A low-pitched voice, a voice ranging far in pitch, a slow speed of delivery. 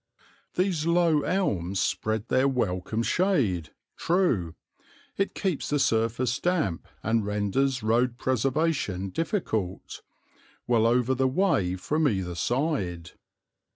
Yes: low, 120 Hz; wide, 7.8 semitones; slow, 110 wpm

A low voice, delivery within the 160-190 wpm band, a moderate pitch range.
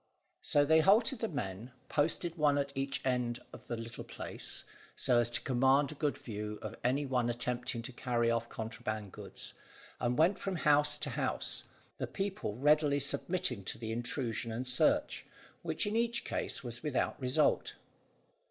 Yes: low, 130 Hz; average, 170 wpm; average, 4.2 semitones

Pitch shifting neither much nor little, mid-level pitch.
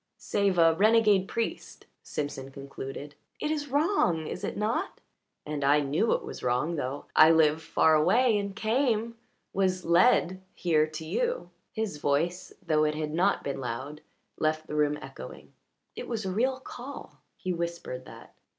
No: wide, 6.4 semitones; medium, 170 Hz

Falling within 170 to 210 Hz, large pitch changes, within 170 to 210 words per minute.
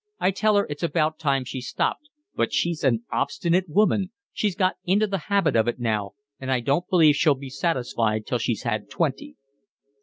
No: medium, 155 Hz; wide, 6.3 semitones; average, 190 wpm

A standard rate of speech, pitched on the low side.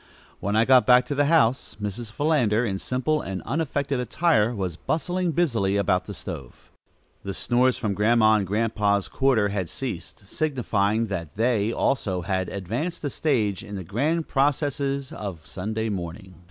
Yes: average, 160 wpm; low, 110 Hz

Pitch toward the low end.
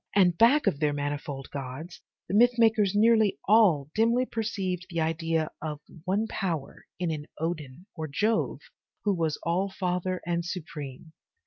No: medium, 175 Hz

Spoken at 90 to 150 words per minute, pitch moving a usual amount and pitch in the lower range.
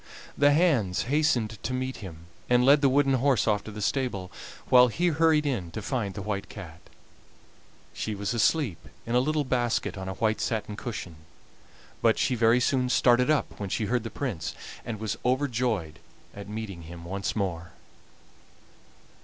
No: average, 170 wpm; average, 4.7 semitones; low, 115 Hz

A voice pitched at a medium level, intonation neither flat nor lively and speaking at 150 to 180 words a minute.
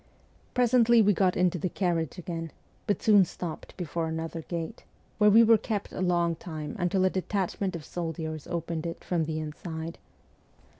Yes: medium, 175 Hz; average, 3.2 semitones; average, 165 wpm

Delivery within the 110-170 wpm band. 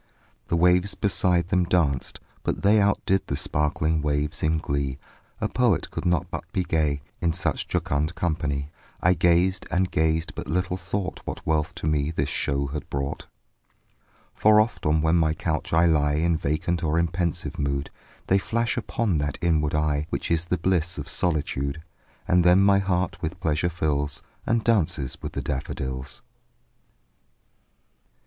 Yes: average, 165 wpm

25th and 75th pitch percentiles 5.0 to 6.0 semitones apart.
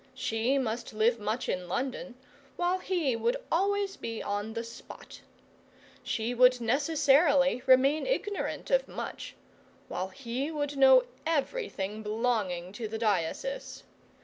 Yes: wide, 5.4 semitones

